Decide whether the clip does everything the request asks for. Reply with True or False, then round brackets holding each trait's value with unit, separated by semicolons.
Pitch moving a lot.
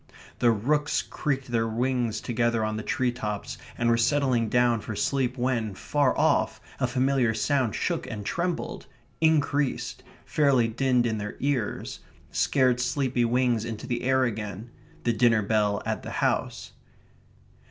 False (2.8 semitones)